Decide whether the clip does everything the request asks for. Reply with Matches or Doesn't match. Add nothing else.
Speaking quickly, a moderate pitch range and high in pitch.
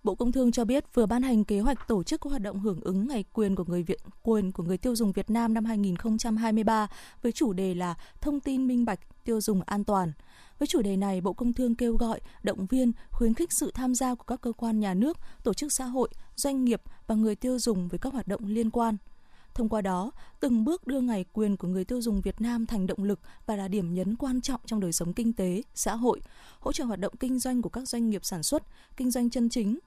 Matches